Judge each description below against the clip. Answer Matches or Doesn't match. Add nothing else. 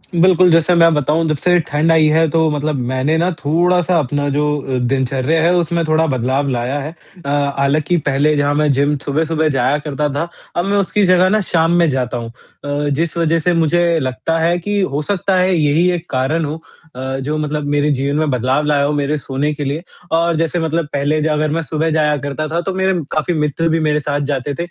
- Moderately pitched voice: Matches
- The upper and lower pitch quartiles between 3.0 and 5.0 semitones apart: Doesn't match